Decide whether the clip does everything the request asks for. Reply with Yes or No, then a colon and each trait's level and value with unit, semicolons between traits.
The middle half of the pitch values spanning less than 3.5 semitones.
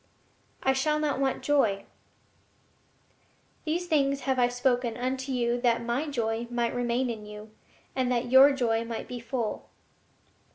Yes: narrow, 2.4 semitones